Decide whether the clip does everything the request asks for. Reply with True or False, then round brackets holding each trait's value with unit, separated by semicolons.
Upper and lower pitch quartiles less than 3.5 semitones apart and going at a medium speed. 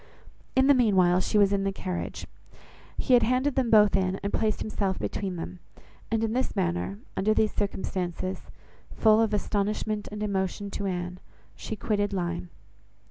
True (2.7 semitones; 165 wpm)